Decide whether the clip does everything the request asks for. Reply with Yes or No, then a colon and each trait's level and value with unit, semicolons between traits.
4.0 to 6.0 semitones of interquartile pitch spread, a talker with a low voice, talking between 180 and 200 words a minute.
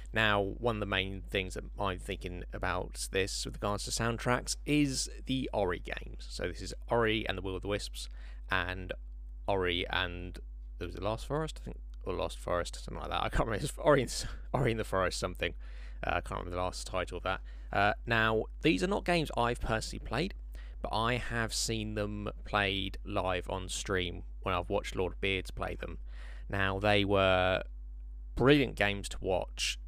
Yes: average, 4.5 semitones; very low, 95 Hz; average, 195 wpm